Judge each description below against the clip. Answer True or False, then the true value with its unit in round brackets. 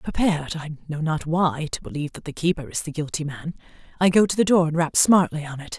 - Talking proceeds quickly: True (220 wpm)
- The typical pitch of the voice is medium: True (160 Hz)